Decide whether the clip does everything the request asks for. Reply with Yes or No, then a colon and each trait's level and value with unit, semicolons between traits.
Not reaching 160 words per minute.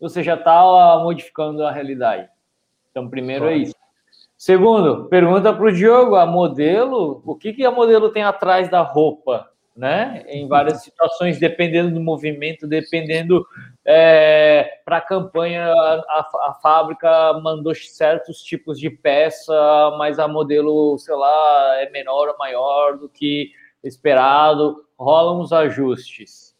Yes: average, 135 wpm